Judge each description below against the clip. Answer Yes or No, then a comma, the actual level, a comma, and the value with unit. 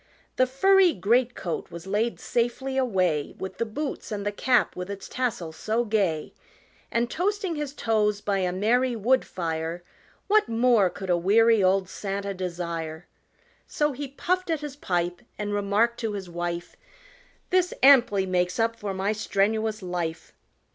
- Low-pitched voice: No, high, 210 Hz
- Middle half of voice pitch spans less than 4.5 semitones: No, wide, 5.4 semitones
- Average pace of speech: Yes, average, 160 wpm